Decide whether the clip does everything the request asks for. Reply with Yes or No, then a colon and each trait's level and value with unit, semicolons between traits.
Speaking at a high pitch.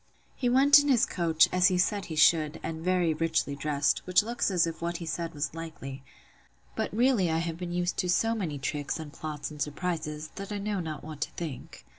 No: medium, 165 Hz